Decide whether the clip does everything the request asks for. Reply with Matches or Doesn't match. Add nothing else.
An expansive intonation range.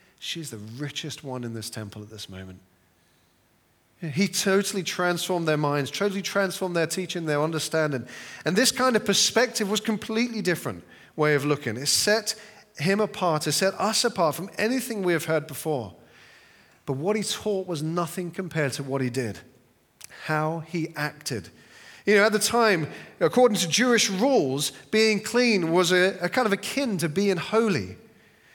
Matches